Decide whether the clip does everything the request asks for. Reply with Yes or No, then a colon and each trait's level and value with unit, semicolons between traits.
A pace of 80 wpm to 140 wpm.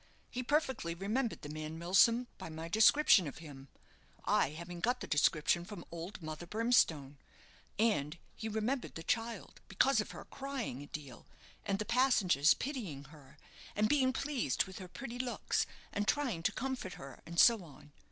No: average, 170 wpm